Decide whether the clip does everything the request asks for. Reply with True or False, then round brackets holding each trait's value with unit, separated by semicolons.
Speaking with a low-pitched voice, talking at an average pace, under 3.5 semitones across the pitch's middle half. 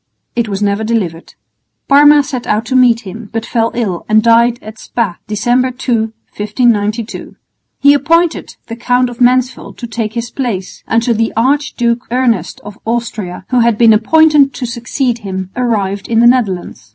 False (235 Hz; 165 wpm; 2.8 semitones)